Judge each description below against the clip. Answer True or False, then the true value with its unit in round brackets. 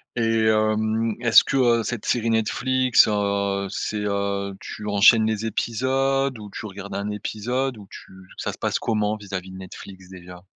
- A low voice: True (110 Hz)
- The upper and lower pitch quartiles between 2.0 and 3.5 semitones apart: True (2.6 semitones)